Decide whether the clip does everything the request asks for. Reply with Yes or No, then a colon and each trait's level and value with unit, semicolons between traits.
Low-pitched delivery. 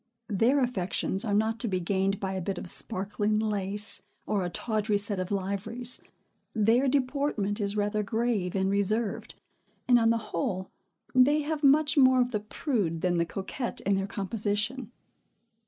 No: high, 210 Hz